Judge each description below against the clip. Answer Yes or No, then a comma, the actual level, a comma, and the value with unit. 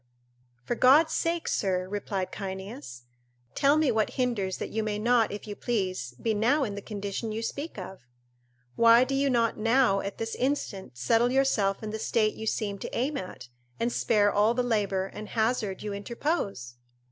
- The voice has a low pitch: No, high, 215 Hz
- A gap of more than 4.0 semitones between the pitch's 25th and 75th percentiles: No, average, 3.6 semitones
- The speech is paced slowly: No, average, 180 wpm